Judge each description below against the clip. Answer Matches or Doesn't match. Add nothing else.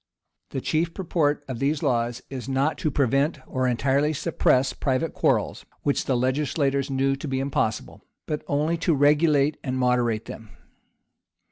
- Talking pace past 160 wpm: Doesn't match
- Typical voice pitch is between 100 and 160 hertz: Matches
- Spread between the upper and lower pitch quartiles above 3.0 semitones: Doesn't match